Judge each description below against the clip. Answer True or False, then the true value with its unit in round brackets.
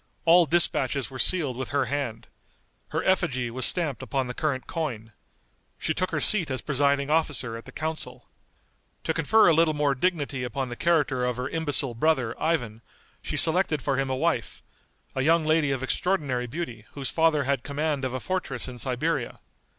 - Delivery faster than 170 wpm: True (180 wpm)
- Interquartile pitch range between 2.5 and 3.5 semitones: False (4.0 semitones)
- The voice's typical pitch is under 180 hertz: True (140 Hz)